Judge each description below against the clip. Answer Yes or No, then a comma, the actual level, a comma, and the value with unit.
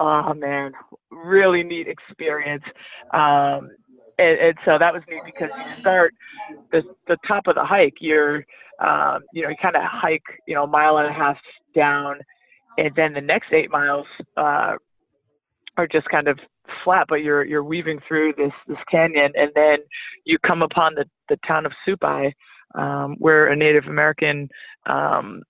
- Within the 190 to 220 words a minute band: No, average, 170 wpm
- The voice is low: No, medium, 155 Hz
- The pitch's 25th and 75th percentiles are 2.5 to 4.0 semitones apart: Yes, average, 2.8 semitones